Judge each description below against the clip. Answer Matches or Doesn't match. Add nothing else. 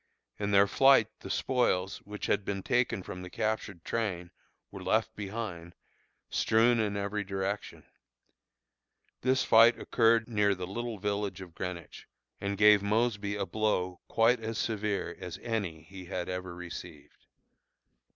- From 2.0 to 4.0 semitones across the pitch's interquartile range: Matches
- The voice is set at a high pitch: Doesn't match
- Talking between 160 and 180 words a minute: Doesn't match